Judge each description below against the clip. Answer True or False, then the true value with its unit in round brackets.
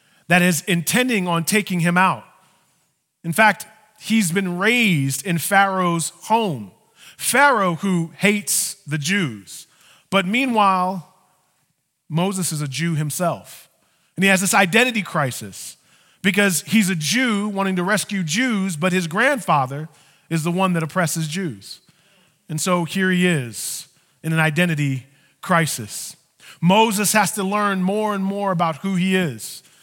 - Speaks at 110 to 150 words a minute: True (140 wpm)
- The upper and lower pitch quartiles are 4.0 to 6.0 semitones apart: False (3.5 semitones)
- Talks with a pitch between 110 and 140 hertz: False (185 Hz)